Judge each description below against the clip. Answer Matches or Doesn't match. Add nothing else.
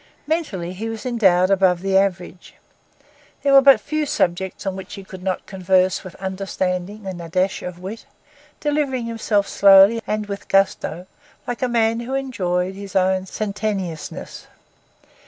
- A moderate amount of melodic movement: Matches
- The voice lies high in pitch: Matches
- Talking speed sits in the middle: Matches